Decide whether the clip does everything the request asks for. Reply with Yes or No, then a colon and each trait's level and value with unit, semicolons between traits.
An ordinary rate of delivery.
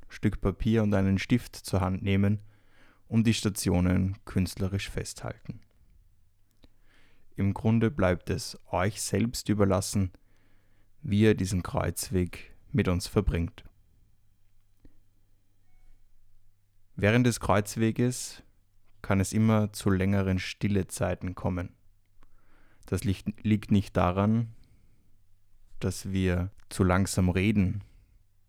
No: slow, 100 wpm